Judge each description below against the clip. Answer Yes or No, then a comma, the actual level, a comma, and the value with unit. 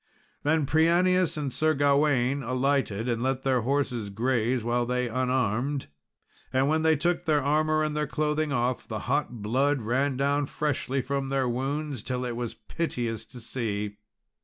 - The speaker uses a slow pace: No, average, 160 wpm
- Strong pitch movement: No, average, 3.4 semitones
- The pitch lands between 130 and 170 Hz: Yes, low, 135 Hz